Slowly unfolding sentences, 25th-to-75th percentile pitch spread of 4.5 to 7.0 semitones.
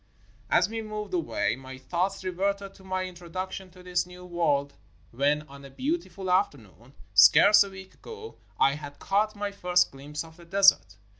No: average, 180 wpm; wide, 5.6 semitones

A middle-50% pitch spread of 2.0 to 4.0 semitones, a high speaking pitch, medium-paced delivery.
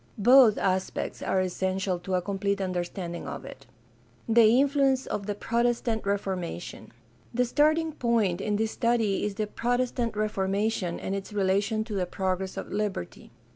Yes: average, 3.7 semitones; high, 205 Hz; average, 160 wpm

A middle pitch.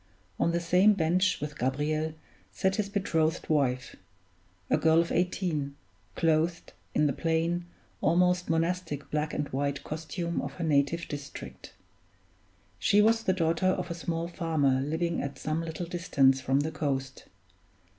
Yes: medium, 160 Hz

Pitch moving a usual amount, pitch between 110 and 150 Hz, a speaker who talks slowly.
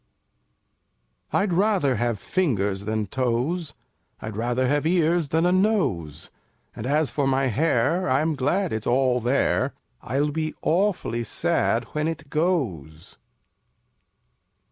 No: wide, 5.9 semitones; medium, 140 Hz; slow, 125 wpm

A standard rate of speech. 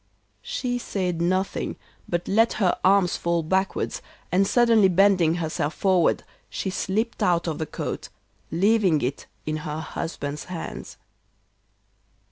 No: slow, 125 wpm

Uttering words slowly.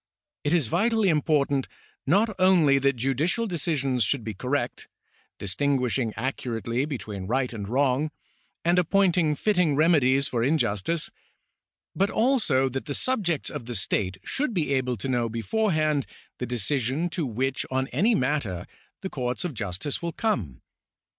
No: average, 145 wpm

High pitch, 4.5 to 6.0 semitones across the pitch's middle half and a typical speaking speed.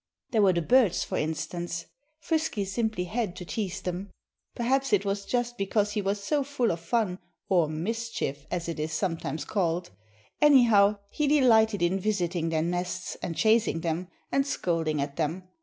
Yes: high, 195 Hz; average, 5.0 semitones; average, 170 wpm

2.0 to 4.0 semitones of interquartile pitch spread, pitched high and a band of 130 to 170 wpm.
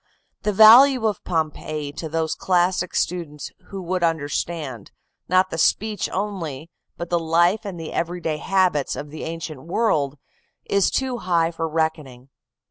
No: average, 3.2 semitones; medium, 170 Hz; average, 150 wpm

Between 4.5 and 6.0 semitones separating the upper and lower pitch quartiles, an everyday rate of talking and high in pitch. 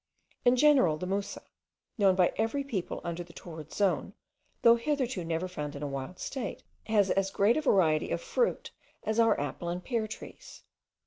Yes: wide, 5.4 semitones; average, 180 wpm; high, 195 Hz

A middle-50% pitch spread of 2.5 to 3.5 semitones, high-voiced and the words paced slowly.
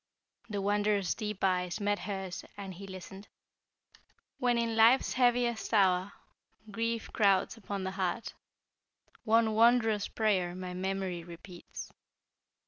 Yes: average, 3.1 semitones; high, 200 Hz; slow, 120 wpm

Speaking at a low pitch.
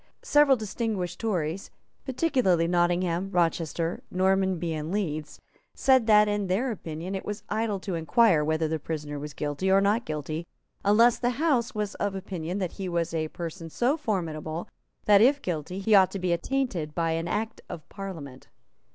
No: medium, 185 Hz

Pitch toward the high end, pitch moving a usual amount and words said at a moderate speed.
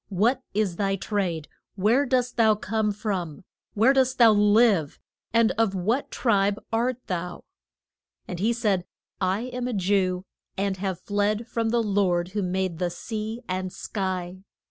Yes: high, 205 Hz; average, 3.4 semitones; average, 155 wpm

